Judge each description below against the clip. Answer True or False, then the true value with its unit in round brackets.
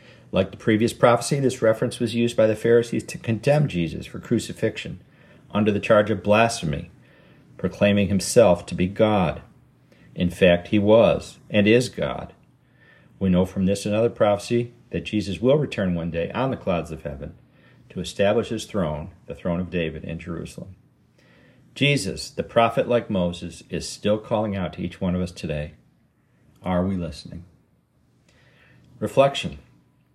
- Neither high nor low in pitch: False (105 Hz)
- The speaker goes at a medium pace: True (160 wpm)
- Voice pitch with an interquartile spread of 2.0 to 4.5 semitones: False (5.2 semitones)